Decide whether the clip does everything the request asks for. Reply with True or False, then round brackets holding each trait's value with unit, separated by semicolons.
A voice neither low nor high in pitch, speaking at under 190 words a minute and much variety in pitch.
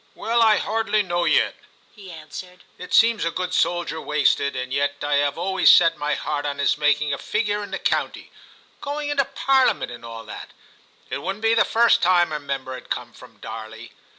False (175 Hz; 205 wpm; 6.7 semitones)